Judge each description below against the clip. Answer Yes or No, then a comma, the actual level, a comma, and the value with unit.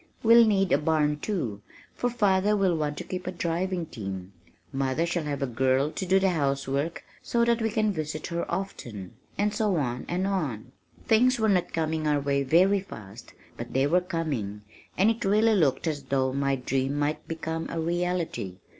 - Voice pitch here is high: No, medium, 160 Hz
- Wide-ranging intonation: Yes, wide, 5.8 semitones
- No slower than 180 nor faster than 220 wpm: Yes, average, 190 wpm